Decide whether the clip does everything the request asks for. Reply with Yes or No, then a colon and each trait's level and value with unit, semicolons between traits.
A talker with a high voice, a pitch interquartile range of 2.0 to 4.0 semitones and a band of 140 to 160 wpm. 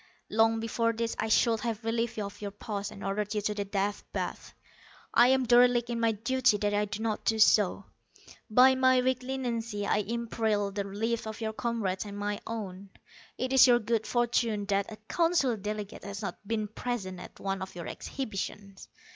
No: high, 220 Hz; narrow, 2.6 semitones; average, 195 wpm